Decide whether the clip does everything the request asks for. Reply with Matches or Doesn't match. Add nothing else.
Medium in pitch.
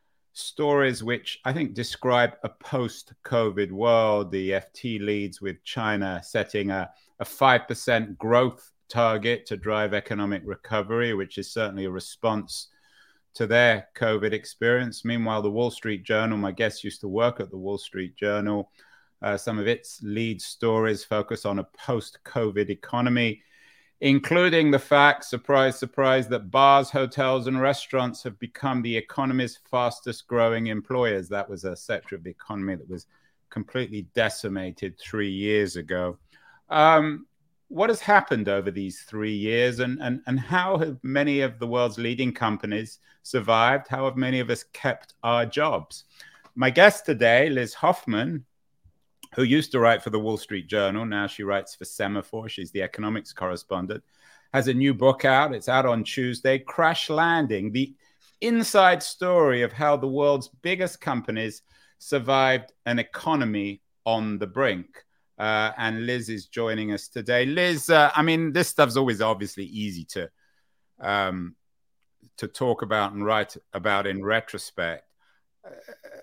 Doesn't match